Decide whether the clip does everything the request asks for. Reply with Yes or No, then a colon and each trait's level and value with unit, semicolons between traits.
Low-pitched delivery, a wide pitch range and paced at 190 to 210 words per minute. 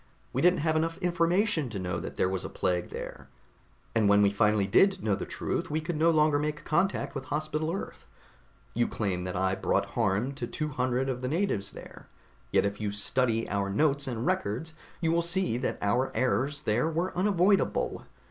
Yes: low, 130 Hz; wide, 7.8 semitones; average, 195 wpm